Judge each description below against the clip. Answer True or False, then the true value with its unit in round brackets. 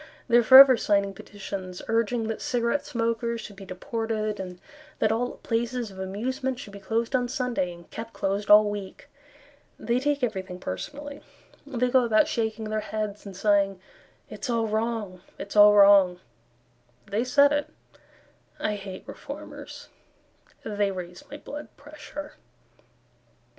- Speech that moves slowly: False (145 wpm)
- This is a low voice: False (220 Hz)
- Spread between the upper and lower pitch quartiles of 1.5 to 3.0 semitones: False (3.6 semitones)